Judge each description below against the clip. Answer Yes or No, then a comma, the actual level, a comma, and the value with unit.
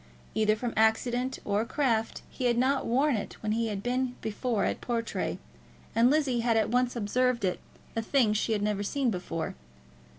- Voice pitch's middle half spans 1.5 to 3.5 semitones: Yes, average, 2.8 semitones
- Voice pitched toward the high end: Yes, high, 230 Hz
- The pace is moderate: Yes, average, 190 wpm